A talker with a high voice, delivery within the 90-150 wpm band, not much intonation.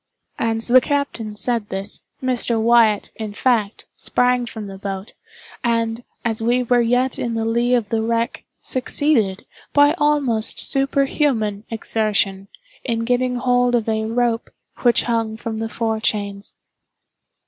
Yes: high, 230 Hz; average, 140 wpm; narrow, 2.2 semitones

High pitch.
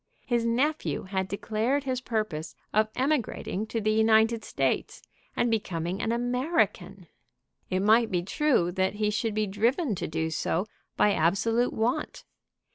Yes: high, 220 Hz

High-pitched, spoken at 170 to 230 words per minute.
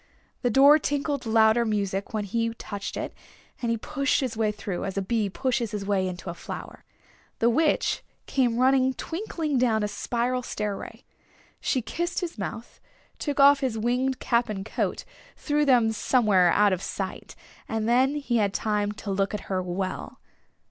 Yes: high, 230 Hz; average, 175 wpm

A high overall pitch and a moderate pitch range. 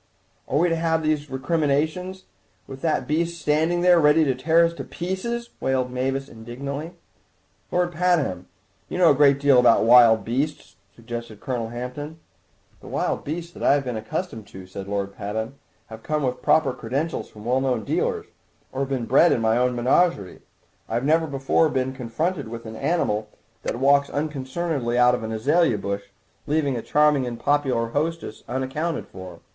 No: low, 135 Hz; average, 5.0 semitones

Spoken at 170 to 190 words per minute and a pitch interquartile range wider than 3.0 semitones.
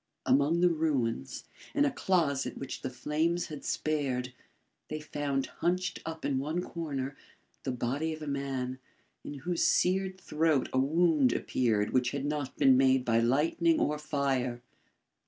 No: average, 155 wpm; average, 3.6 semitones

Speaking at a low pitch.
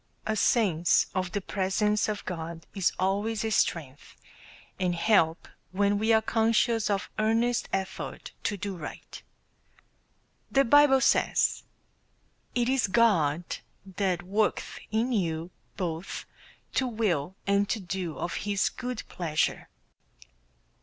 No: high, 200 Hz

